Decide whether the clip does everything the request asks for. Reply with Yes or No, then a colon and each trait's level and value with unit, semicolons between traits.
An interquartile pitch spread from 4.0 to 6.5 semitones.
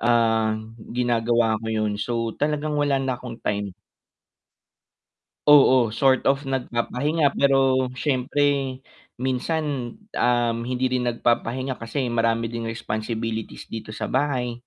No: average, 2.7 semitones